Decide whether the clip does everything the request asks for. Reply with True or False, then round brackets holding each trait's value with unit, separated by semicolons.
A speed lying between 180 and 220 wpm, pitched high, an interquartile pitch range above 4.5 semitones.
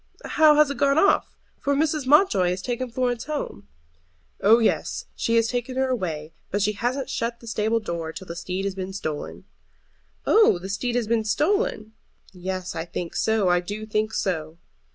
True (185 wpm; 220 Hz; 5.6 semitones)